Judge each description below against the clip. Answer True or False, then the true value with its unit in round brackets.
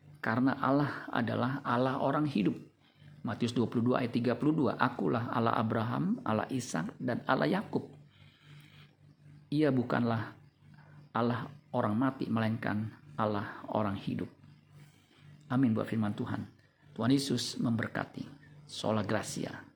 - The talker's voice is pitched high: False (130 Hz)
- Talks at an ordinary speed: True (110 wpm)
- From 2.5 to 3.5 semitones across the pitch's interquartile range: False (4.0 semitones)